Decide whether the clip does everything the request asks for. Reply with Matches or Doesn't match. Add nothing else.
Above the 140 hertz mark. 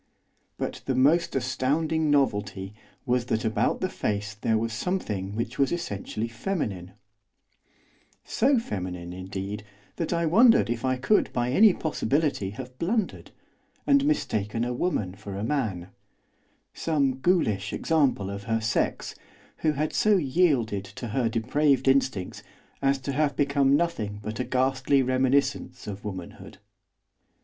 Doesn't match